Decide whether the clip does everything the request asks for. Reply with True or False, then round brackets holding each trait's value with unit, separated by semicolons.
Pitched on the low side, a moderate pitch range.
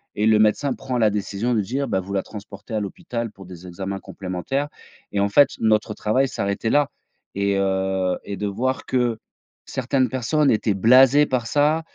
True (110 Hz; 4.7 semitones)